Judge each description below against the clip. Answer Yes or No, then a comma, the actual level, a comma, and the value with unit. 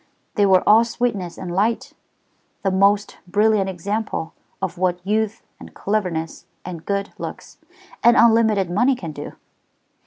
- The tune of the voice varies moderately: Yes, average, 3.3 semitones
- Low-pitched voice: No, high, 200 Hz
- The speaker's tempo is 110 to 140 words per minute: Yes, slow, 135 wpm